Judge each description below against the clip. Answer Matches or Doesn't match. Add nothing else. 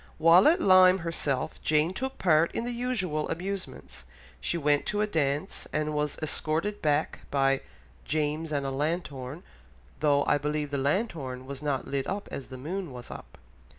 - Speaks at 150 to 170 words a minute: Matches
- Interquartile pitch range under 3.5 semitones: Doesn't match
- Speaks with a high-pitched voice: Doesn't match